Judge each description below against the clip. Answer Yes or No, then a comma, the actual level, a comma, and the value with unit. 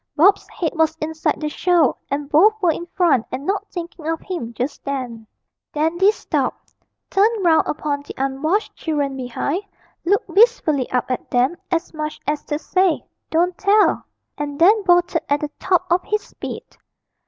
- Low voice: No, very high, 320 Hz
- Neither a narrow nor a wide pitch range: Yes, average, 4.3 semitones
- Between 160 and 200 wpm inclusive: Yes, average, 165 wpm